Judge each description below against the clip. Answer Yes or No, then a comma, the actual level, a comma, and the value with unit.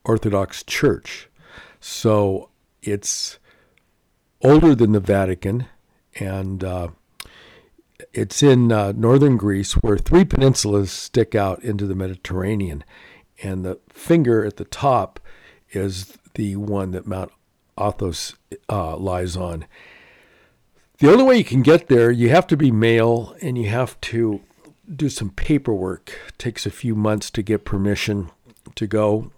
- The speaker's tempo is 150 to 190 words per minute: No, slow, 135 wpm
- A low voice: Yes, low, 105 Hz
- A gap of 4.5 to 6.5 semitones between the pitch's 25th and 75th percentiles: No, average, 3.8 semitones